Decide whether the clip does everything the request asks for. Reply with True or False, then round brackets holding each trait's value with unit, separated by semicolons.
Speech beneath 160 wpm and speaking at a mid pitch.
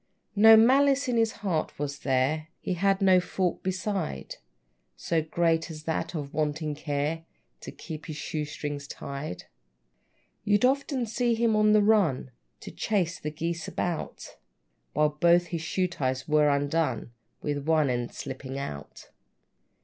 True (150 wpm; 160 Hz)